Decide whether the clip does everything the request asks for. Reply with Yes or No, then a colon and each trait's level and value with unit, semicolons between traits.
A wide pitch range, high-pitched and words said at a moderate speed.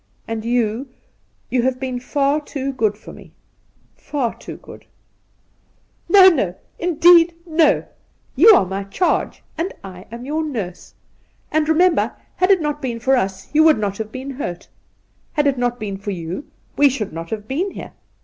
Yes: wide, 6.4 semitones; very high, 260 Hz; average, 185 wpm